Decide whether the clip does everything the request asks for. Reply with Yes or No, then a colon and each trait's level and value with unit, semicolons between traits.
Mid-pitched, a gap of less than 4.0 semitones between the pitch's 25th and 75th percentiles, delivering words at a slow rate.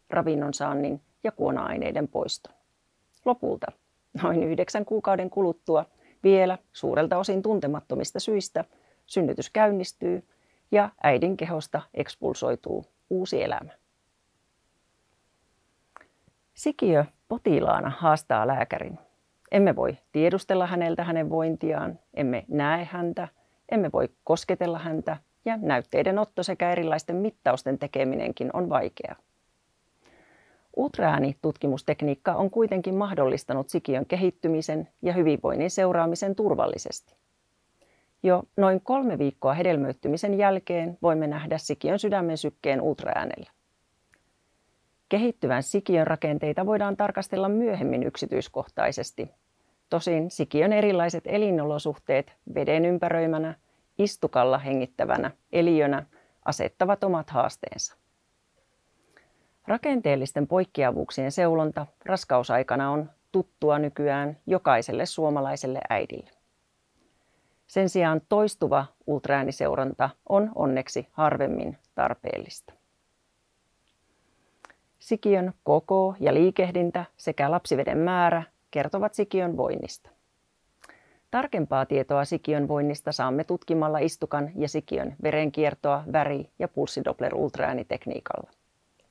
No: medium, 165 Hz; average, 4.3 semitones; slow, 90 wpm